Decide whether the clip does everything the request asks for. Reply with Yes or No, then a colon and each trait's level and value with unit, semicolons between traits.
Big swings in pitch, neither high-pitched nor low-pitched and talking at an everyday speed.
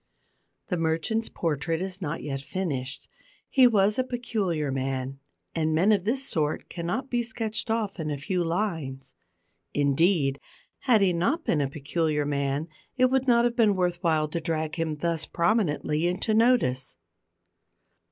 Yes: wide, 6.4 semitones; medium, 170 Hz; average, 155 wpm